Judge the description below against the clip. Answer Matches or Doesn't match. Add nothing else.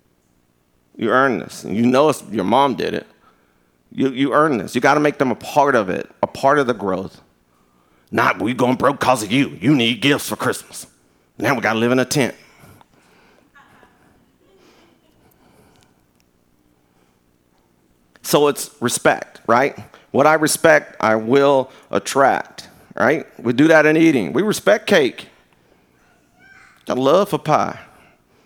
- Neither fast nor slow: Matches